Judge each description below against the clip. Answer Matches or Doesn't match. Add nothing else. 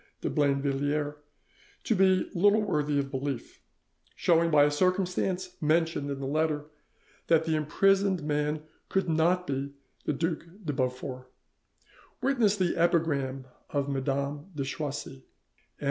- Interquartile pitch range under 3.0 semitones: Doesn't match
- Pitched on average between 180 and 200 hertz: Doesn't match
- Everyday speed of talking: Doesn't match